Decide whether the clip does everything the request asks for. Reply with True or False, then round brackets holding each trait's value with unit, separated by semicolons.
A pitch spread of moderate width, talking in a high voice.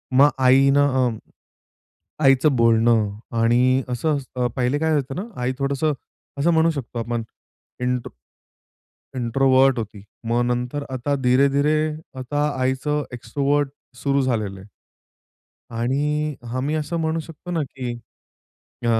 False (3.1 semitones; 135 Hz)